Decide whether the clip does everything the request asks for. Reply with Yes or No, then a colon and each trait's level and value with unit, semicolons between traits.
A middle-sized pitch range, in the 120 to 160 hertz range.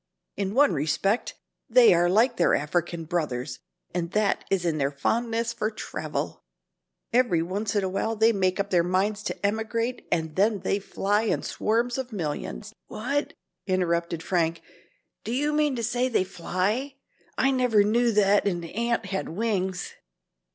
No: average, 4.7 semitones; high, 200 Hz